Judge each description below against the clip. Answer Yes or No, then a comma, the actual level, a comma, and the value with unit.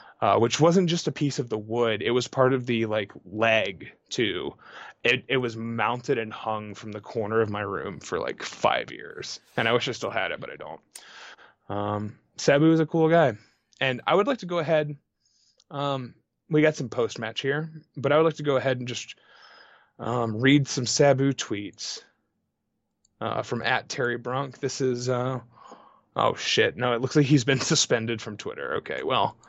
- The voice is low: Yes, low, 130 Hz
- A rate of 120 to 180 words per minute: No, average, 200 wpm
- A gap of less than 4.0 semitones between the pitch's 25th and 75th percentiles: No, average, 4.5 semitones